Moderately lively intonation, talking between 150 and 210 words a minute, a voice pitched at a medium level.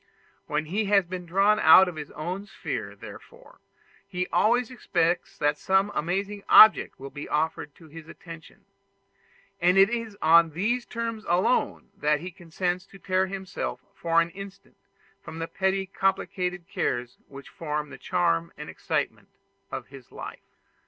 Yes: average, 3.8 semitones; average, 160 wpm; medium, 180 Hz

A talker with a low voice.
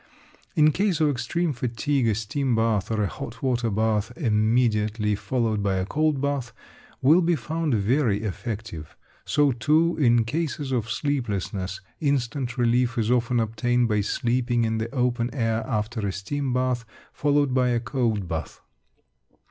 Yes: low, 120 Hz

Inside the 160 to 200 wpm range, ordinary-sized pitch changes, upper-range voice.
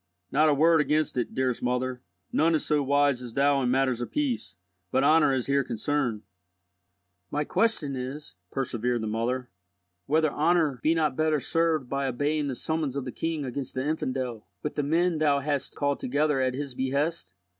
No: average, 185 wpm; average, 3.2 semitones; medium, 140 Hz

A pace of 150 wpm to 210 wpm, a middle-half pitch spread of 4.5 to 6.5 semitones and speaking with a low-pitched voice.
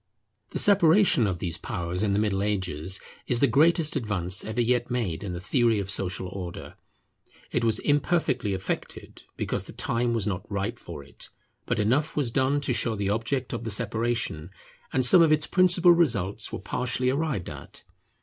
Yes: average, 180 wpm; wide, 5.5 semitones; low, 115 Hz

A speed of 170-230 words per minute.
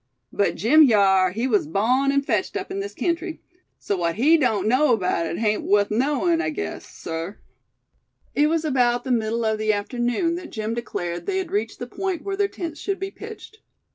Yes: average, 200 wpm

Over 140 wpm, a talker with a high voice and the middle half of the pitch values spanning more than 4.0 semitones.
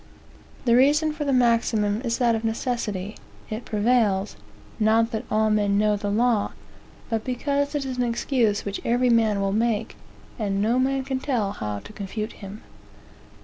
No: average, 170 wpm; high, 225 Hz; average, 3.2 semitones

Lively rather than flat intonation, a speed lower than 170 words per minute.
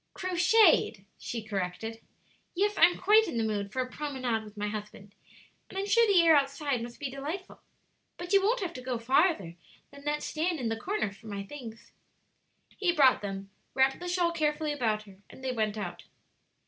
No: wide, 7.9 semitones; average, 190 wpm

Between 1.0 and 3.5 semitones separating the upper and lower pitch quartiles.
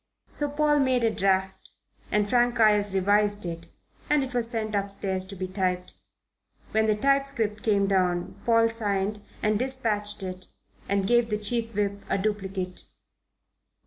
Yes: average, 3.0 semitones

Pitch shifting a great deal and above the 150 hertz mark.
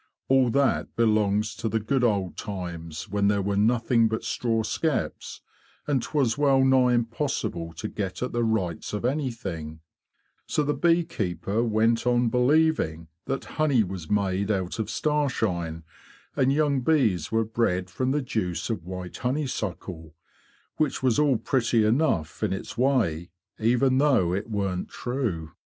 No: wide, 5.8 semitones; low, 115 Hz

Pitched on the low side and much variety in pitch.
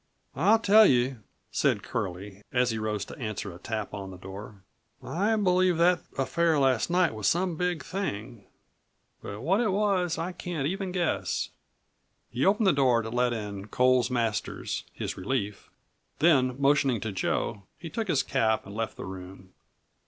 Yes: low, 130 Hz; wide, 8.7 semitones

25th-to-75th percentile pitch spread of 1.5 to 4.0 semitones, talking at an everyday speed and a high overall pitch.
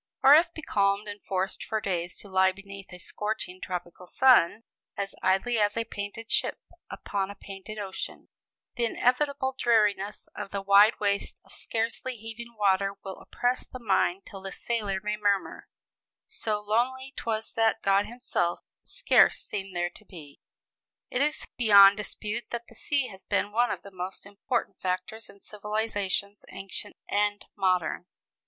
Yes: average, 2.8 semitones; average, 160 wpm; high, 205 Hz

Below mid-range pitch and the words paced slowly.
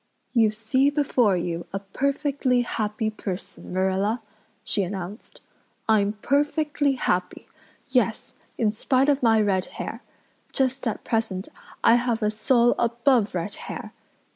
No: high, 225 Hz; slow, 130 wpm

